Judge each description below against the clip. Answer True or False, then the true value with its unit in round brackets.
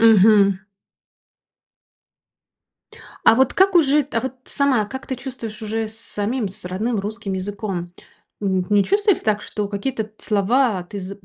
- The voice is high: True (215 Hz)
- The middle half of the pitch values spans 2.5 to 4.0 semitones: False (4.4 semitones)